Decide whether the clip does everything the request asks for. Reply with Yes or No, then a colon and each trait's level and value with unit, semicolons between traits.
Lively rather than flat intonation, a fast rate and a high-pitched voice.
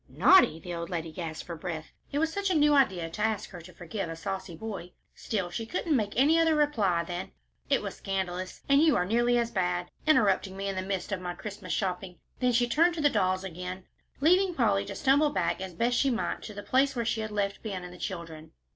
Yes: wide, 5.8 semitones; fast, 235 wpm; high, 200 Hz